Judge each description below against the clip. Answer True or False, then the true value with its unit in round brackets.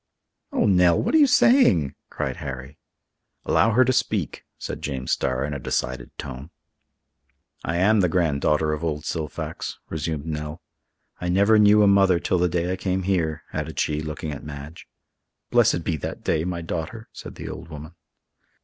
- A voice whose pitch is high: False (80 Hz)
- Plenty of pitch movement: False (3.8 semitones)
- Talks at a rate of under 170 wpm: False (175 wpm)